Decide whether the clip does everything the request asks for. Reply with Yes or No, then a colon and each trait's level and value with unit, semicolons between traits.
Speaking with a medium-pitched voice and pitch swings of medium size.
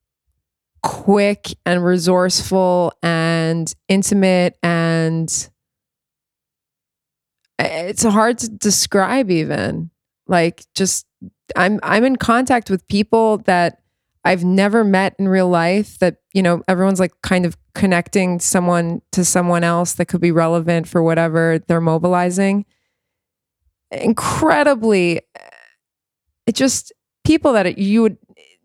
Yes: medium, 180 Hz; average, 3.2 semitones